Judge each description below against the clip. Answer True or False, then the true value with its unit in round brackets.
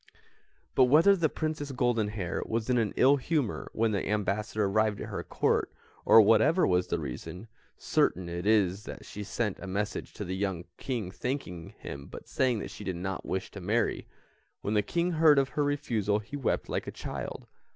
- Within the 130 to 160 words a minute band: False (195 wpm)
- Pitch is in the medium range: False (110 Hz)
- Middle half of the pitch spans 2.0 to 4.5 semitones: False (5.3 semitones)